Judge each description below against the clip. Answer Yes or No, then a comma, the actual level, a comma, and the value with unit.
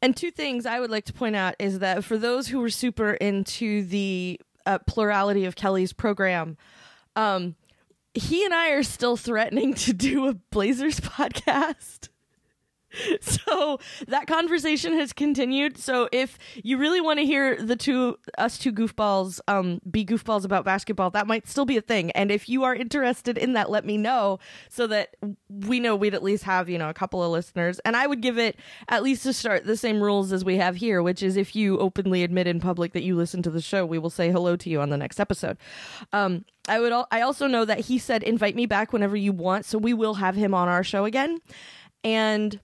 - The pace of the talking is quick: Yes, fast, 215 wpm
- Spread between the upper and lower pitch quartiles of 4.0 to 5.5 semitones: Yes, average, 4.6 semitones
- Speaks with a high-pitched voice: Yes, high, 215 Hz